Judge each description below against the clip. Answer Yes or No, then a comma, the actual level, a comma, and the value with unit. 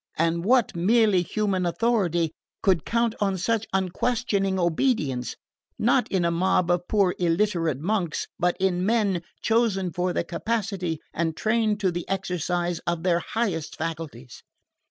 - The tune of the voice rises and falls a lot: No, average, 3.9 semitones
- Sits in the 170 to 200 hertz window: Yes, medium, 185 Hz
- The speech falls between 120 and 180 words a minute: Yes, average, 140 wpm